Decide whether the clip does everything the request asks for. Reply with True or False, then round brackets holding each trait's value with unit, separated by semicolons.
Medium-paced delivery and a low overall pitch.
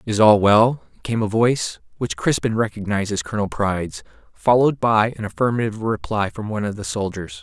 True (180 wpm; 110 Hz)